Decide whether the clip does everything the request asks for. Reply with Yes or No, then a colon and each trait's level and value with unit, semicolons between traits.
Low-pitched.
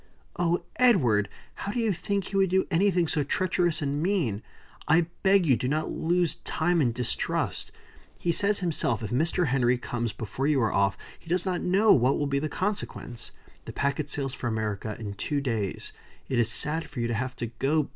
No: medium, 150 Hz